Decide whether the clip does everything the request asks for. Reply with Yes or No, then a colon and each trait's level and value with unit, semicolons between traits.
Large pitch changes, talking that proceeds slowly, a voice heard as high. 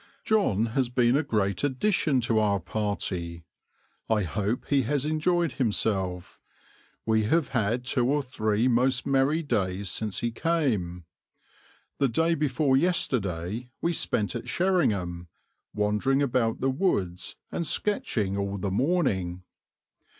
No: wide, 6.0 semitones; slow, 130 wpm; low, 120 Hz